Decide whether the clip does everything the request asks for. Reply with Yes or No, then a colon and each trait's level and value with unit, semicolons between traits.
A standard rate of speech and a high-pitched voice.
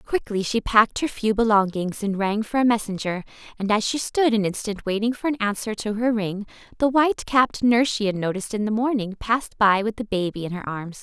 No: fast, 230 wpm; high, 215 Hz